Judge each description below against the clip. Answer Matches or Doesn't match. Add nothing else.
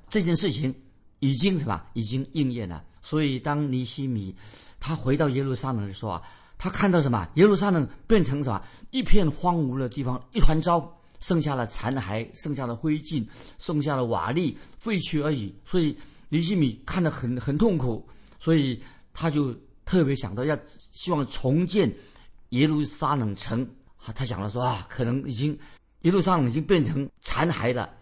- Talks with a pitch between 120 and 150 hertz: Matches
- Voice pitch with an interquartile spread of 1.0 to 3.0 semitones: Doesn't match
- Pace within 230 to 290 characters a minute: Matches